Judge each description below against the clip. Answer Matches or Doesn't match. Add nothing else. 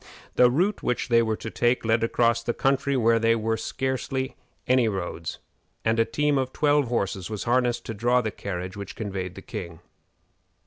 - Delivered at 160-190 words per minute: Matches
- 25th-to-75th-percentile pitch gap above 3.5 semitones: Doesn't match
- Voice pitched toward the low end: Matches